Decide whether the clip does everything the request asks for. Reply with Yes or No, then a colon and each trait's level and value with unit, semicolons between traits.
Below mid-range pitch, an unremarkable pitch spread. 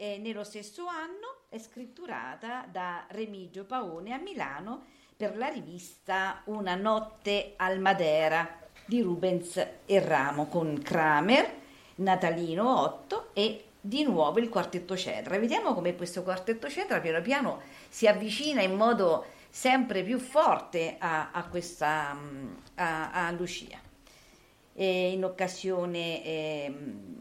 No: high, 190 Hz; average, 5.0 semitones